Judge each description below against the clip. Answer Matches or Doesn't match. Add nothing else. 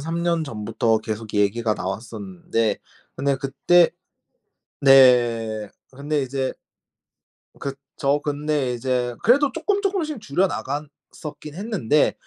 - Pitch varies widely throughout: Matches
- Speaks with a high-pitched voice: Doesn't match